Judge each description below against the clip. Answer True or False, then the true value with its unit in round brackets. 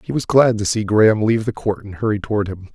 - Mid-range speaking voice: False (105 Hz)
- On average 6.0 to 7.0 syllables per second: True (6.9 syllables/s)